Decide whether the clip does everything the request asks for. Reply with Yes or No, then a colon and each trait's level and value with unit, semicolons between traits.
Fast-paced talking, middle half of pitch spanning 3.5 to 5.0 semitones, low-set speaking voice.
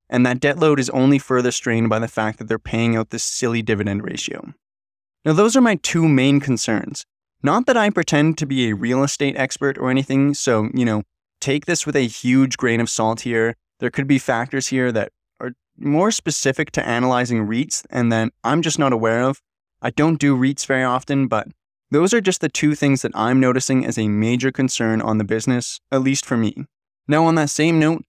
Yes: fast, 215 wpm; average, 3.8 semitones; low, 130 Hz